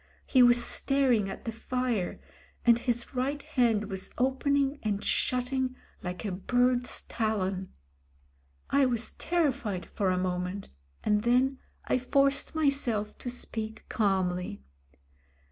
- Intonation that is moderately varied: Yes, average, 4.5 semitones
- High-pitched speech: Yes, high, 240 Hz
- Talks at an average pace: No, slow, 125 wpm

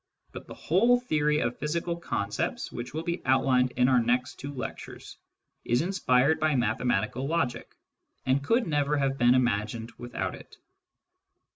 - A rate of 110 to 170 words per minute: Yes, average, 155 wpm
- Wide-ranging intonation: No, average, 4.4 semitones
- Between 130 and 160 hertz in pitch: Yes, low, 135 Hz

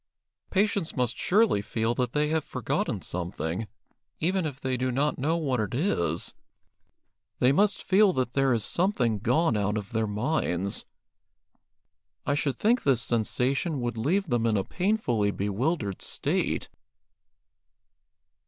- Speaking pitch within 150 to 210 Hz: No, low, 130 Hz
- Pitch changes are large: Yes, wide, 6.6 semitones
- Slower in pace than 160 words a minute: Yes, average, 140 wpm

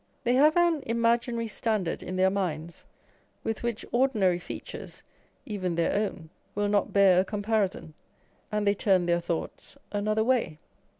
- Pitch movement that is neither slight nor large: Yes, average, 4.0 semitones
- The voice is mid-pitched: No, high, 205 Hz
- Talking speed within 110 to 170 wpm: Yes, average, 145 wpm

